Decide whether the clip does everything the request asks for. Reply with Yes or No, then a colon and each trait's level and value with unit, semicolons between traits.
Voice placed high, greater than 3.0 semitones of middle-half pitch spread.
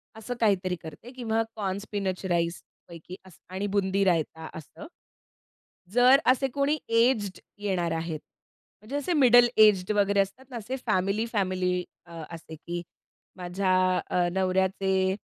Yes: high, 195 Hz; average, 3.8 semitones